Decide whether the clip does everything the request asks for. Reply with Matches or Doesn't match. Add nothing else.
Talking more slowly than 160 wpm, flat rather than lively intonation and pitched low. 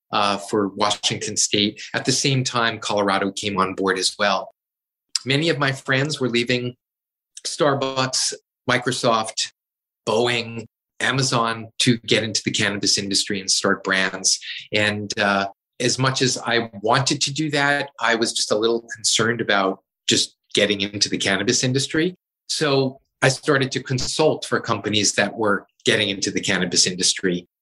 Doesn't match